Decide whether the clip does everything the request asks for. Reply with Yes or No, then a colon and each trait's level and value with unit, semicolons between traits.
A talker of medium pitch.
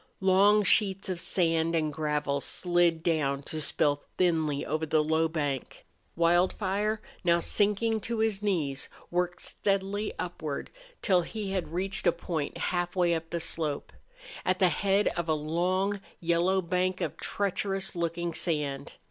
Yes: medium, 175 Hz